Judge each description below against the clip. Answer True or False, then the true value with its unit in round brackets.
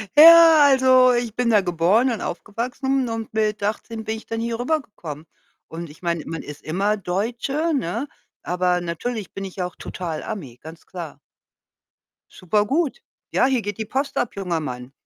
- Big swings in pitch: True (6.0 semitones)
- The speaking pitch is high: True (215 Hz)